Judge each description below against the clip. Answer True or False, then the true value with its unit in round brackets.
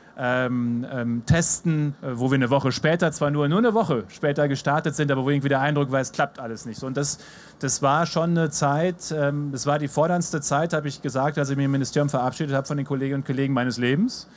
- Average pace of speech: False (240 wpm)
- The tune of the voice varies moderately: False (2.2 semitones)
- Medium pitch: True (145 Hz)